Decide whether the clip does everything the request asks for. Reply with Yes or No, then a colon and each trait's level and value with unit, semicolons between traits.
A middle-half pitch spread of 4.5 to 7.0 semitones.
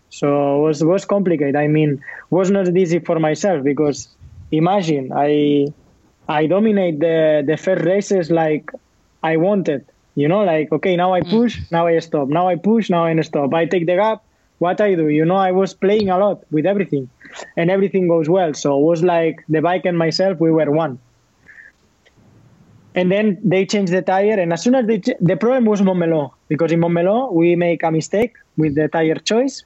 No: average, 3.7 semitones